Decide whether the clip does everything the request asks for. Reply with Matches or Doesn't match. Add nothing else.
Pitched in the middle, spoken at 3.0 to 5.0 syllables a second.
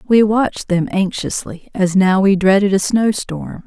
Doesn't match